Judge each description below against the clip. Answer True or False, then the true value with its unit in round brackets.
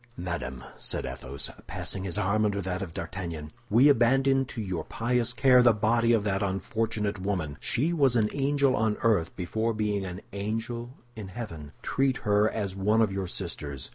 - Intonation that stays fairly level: False (3.9 semitones)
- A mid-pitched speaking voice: False (105 Hz)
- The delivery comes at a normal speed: True (175 wpm)